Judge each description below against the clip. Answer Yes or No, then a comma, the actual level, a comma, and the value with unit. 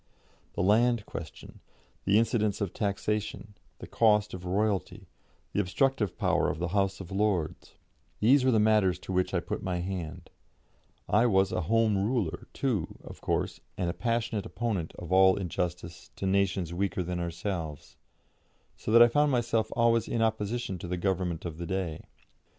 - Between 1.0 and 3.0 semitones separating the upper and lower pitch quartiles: No, average, 3.7 semitones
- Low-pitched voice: Yes, low, 100 Hz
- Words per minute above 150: Yes, average, 165 wpm